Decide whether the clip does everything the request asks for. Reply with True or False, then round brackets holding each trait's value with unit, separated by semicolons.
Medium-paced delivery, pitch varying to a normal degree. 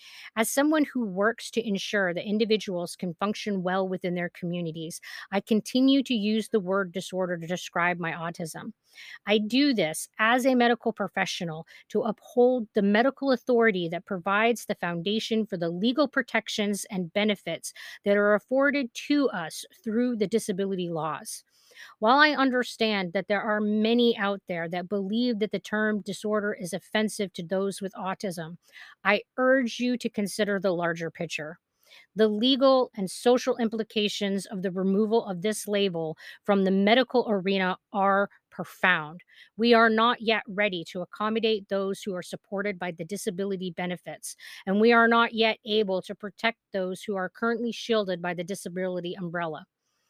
True (160 wpm; 3.5 semitones)